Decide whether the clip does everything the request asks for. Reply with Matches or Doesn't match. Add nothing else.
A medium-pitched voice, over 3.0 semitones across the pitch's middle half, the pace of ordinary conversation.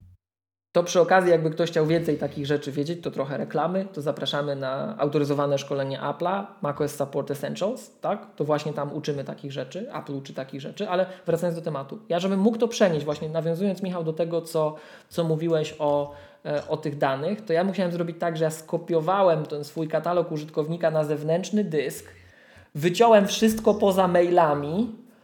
Doesn't match